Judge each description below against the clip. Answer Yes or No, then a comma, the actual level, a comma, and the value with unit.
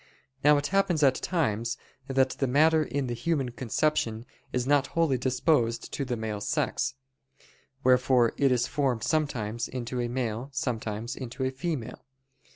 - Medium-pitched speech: No, low, 130 Hz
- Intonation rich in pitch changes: No, average, 3.4 semitones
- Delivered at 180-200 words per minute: No, average, 155 wpm